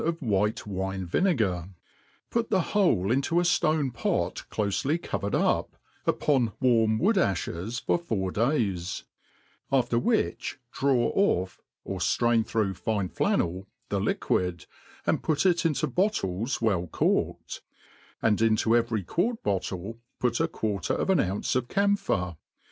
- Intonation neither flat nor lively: No, wide, 8.2 semitones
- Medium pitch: No, low, 115 Hz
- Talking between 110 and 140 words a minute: Yes, slow, 135 wpm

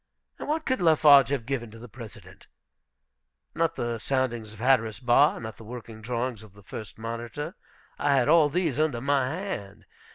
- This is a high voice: No, low, 125 Hz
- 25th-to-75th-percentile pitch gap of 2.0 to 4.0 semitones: No, average, 4.5 semitones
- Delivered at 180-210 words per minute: No, average, 170 wpm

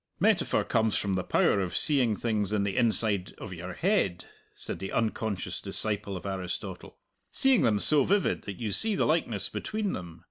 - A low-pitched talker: Yes, low, 105 Hz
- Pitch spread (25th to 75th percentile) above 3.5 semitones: Yes, average, 4.4 semitones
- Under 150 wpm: No, average, 180 wpm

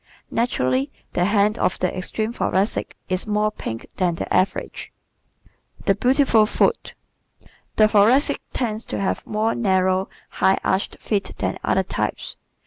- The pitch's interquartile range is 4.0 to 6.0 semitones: No, average, 3.0 semitones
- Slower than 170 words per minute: Yes, average, 140 wpm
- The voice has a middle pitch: No, high, 205 Hz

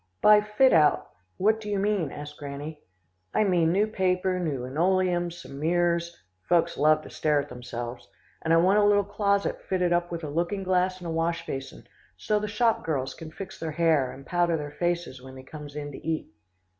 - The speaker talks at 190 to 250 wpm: Yes, fast, 205 wpm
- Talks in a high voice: No, medium, 170 Hz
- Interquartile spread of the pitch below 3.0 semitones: No, average, 4.2 semitones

